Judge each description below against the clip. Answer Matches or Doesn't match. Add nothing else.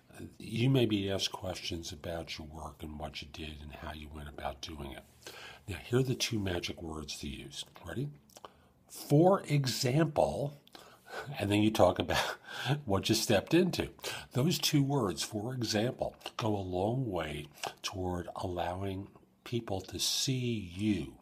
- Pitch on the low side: Matches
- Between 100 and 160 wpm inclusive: Matches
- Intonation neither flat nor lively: Doesn't match